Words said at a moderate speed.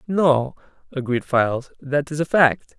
Yes: average, 150 wpm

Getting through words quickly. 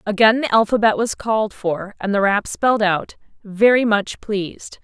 No: average, 175 wpm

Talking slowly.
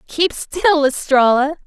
Yes: slow, 110 wpm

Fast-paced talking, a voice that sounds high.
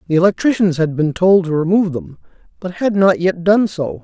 No: fast, 210 wpm; medium, 180 Hz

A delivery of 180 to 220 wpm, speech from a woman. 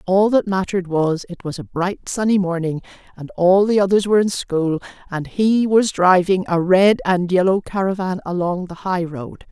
Yes: average, 190 wpm; female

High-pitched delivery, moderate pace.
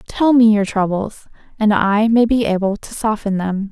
Yes: high, 210 Hz; average, 195 wpm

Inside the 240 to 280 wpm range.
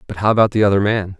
No: fast, 300 wpm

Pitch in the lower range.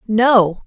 No: high, 215 Hz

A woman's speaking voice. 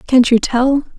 Yes: female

